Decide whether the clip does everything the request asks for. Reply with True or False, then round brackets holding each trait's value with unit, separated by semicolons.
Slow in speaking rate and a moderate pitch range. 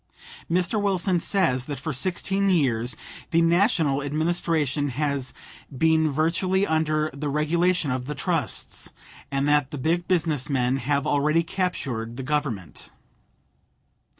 True (125 wpm; 3.7 semitones)